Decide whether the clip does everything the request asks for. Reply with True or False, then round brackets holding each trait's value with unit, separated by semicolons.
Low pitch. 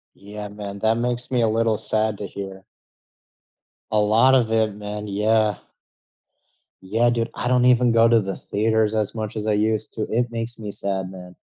True (110 Hz)